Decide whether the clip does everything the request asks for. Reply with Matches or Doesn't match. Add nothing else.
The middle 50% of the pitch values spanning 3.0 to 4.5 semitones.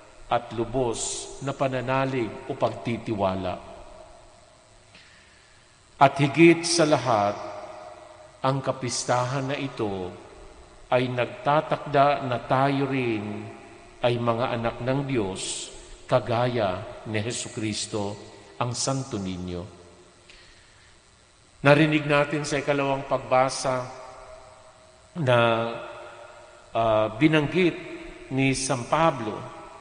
Matches